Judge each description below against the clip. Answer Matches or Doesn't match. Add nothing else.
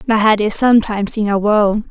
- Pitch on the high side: Matches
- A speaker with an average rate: Doesn't match